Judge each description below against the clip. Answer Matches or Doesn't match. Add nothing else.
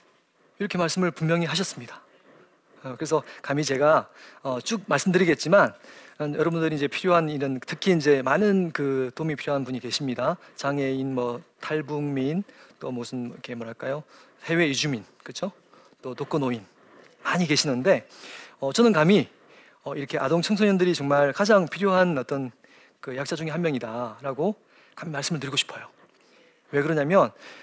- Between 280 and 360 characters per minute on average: Matches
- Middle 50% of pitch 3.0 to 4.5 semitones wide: Matches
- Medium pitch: Matches